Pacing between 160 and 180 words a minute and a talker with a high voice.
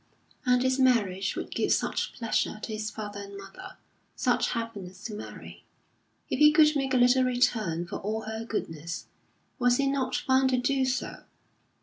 Yes: average, 170 wpm; high, 235 Hz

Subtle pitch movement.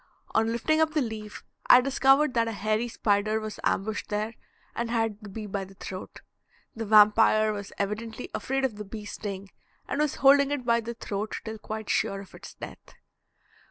Yes: narrow, 2.3 semitones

